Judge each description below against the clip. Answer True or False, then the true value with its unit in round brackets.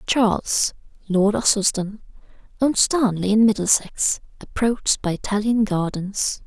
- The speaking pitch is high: True (210 Hz)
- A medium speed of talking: False (100 wpm)